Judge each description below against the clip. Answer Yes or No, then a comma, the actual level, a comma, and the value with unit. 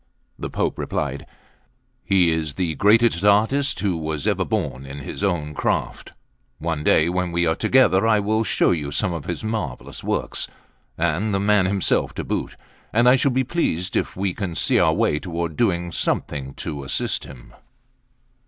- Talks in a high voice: No, very low, 90 Hz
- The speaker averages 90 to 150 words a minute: No, average, 175 wpm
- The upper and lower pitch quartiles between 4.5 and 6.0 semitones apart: Yes, average, 5.0 semitones